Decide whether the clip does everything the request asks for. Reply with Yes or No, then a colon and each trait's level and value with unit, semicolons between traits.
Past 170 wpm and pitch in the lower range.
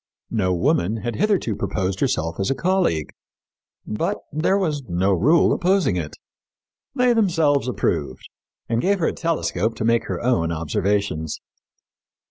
No: average, 140 wpm; low, 115 Hz